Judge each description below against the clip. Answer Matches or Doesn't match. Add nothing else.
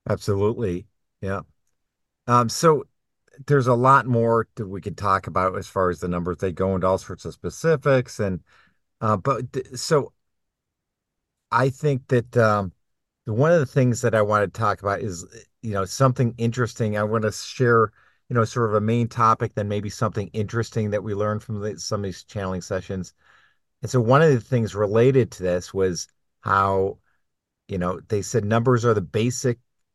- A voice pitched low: Matches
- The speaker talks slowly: Doesn't match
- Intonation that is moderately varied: Matches